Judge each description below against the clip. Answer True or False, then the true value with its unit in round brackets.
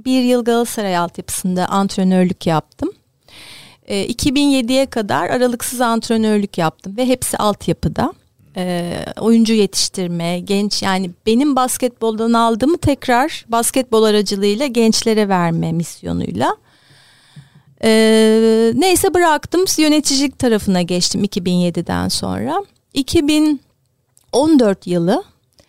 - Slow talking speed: True (85 wpm)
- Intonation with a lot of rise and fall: True (6.1 semitones)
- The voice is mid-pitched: False (220 Hz)